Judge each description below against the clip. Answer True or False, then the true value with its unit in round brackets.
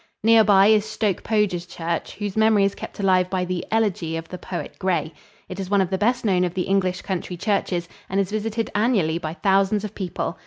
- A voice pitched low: False (195 Hz)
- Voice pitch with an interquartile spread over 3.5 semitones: False (2.7 semitones)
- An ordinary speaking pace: False (220 wpm)